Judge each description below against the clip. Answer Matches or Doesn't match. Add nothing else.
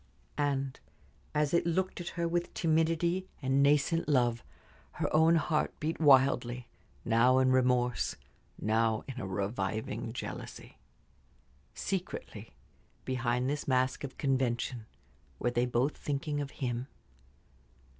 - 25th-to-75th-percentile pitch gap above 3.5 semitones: Matches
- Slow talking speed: Matches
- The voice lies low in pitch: Matches